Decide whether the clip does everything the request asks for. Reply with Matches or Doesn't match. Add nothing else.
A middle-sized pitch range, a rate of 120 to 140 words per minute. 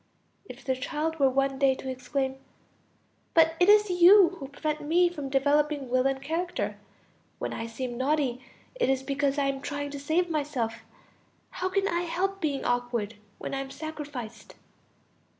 Doesn't match